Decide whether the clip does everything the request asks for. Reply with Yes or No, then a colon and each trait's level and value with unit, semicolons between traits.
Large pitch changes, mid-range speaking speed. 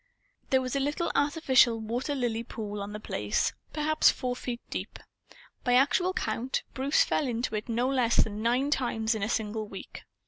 No: average, 3.5 semitones; average, 180 wpm